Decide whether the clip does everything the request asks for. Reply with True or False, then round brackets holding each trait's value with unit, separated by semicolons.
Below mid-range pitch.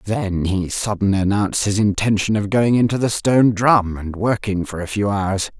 True (105 Hz)